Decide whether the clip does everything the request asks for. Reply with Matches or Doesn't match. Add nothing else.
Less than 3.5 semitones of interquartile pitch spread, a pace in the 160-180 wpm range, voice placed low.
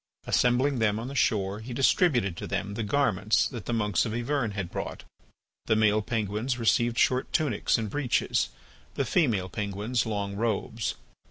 Matches